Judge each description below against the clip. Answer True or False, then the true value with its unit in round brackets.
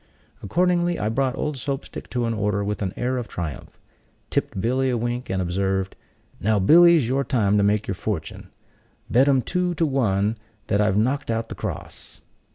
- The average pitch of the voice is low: True (115 Hz)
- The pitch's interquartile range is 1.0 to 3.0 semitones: False (5.1 semitones)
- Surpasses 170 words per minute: True (190 wpm)